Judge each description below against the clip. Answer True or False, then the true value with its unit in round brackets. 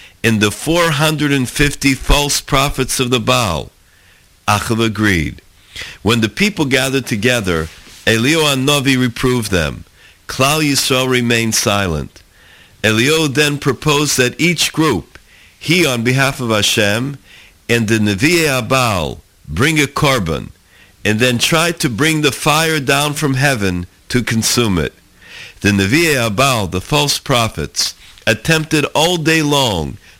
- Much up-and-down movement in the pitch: True (5.9 semitones)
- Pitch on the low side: True (125 Hz)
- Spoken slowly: True (130 wpm)